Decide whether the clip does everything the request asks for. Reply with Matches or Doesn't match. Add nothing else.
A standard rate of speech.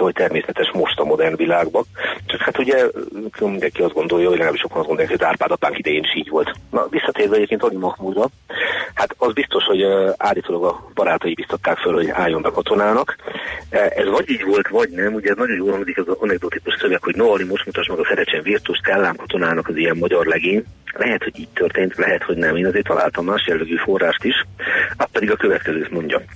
Doesn't match